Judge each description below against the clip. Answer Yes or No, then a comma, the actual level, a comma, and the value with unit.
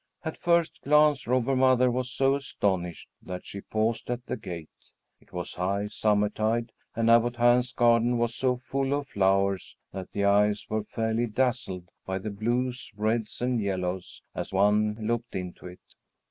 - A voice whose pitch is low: Yes, low, 115 Hz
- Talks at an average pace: Yes, average, 160 wpm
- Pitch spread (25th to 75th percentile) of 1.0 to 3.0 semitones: No, average, 3.8 semitones